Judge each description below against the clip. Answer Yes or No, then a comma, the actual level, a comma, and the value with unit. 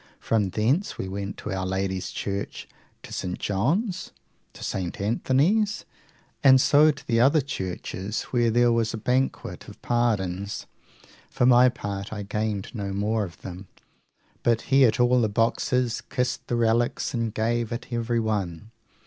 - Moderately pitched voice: No, low, 115 Hz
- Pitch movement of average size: Yes, average, 3.8 semitones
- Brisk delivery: No, average, 155 wpm